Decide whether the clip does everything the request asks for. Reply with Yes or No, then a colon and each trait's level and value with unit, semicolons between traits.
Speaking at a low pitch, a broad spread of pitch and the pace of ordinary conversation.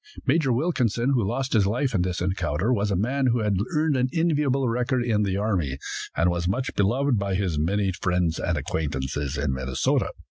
Yes: low, 105 Hz; wide, 6.4 semitones; average, 190 wpm